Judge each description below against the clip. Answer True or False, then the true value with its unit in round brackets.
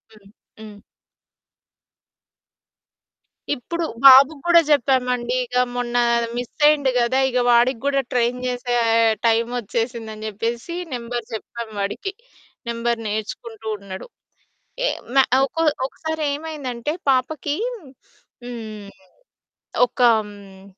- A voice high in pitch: True (245 Hz)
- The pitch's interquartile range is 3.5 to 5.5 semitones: False (2.9 semitones)